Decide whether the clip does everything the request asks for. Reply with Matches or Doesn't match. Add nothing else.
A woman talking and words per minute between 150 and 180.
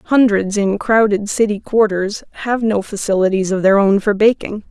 Matches